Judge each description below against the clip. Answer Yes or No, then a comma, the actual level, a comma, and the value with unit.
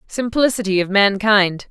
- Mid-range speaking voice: No, high, 210 Hz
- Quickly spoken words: No, slow, 105 wpm